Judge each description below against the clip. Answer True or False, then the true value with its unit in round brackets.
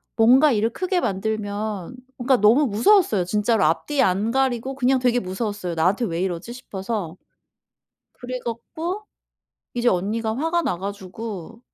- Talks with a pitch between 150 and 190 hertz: False (225 Hz)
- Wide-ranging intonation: False (4.5 semitones)